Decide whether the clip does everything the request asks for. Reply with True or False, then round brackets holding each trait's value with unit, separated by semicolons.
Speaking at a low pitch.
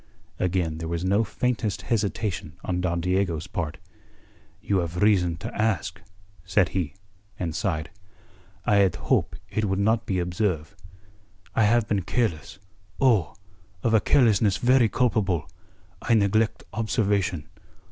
True (100 Hz)